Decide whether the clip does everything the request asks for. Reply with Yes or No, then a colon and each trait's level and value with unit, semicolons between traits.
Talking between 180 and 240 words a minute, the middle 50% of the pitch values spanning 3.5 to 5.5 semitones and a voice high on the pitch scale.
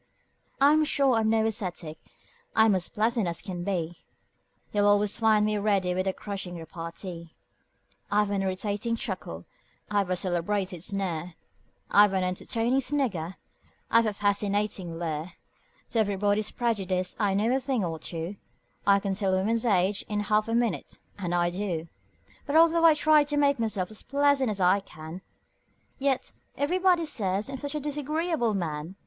No: average, 160 wpm; average, 4.2 semitones; high, 205 Hz